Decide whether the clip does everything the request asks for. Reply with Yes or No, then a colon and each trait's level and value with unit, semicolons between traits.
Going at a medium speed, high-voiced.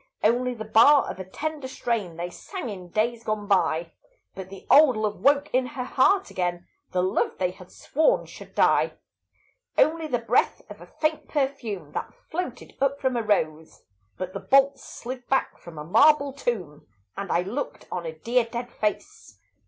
Yes: average, 180 wpm; high, 230 Hz